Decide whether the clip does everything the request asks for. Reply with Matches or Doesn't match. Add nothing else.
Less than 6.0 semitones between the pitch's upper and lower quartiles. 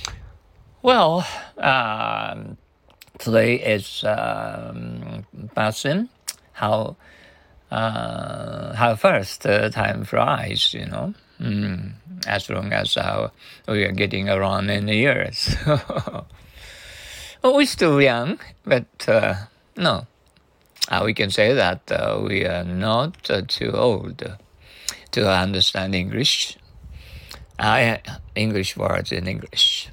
Doesn't match